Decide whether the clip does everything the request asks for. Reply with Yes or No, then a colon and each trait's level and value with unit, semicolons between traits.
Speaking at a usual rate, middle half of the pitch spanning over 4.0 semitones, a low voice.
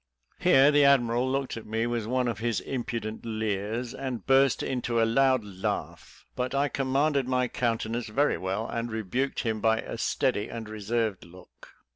No: average, 170 wpm; average, 3.0 semitones; low, 120 Hz